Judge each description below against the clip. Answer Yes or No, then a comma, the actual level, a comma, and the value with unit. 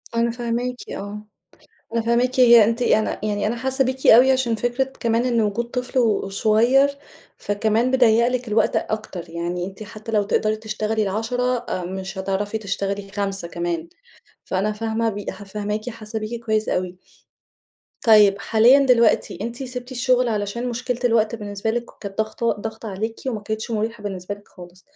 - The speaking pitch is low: No, high, 220 Hz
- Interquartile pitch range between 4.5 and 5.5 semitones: No, average, 2.7 semitones